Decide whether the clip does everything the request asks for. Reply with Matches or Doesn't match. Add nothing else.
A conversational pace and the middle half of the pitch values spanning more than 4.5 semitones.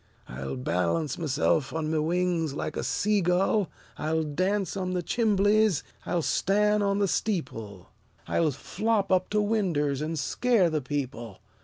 Matches